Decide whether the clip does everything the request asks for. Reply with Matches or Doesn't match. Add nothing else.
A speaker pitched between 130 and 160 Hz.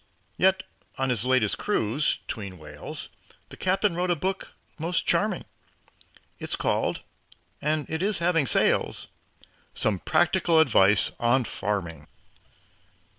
Matches